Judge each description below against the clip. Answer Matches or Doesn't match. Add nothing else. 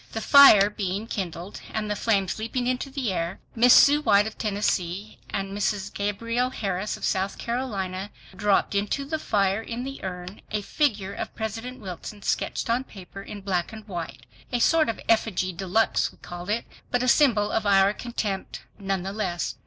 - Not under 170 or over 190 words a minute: Matches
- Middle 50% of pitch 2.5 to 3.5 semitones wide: Matches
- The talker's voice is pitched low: Doesn't match